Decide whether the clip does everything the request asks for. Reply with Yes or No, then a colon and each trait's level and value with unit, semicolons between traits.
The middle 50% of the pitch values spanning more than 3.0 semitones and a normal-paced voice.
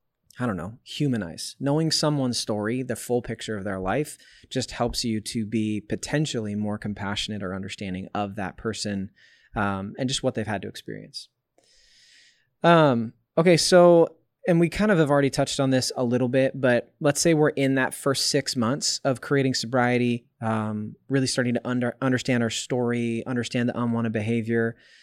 Yes: average, 3.8 semitones; average, 175 wpm